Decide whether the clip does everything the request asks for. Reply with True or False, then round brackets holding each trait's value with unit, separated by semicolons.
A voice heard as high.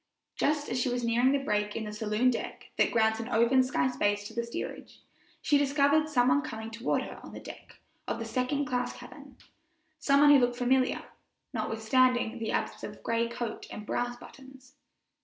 True (245 Hz)